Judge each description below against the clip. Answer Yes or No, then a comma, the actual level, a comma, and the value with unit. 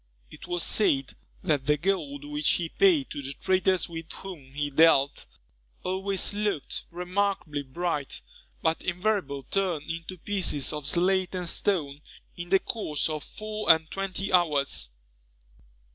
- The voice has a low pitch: No, medium, 170 Hz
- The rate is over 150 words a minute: No, average, 140 wpm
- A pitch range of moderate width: Yes, average, 4.6 semitones